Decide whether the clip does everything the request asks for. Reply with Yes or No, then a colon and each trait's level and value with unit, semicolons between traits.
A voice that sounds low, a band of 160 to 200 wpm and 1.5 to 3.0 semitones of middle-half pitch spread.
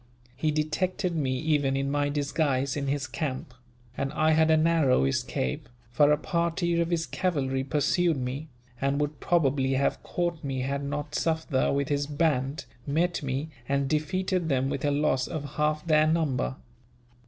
No: medium, 145 Hz; average, 165 wpm; average, 2.7 semitones